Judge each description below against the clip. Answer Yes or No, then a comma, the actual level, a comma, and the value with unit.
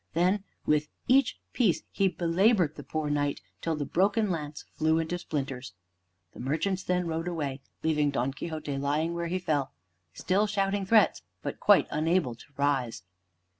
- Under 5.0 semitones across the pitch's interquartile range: Yes, average, 4.3 semitones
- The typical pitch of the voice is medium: Yes, medium, 160 Hz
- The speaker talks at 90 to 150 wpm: No, average, 160 wpm